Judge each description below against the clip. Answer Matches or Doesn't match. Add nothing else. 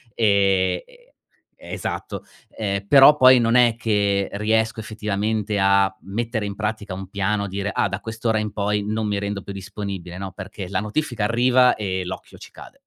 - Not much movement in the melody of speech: Matches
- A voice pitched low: Matches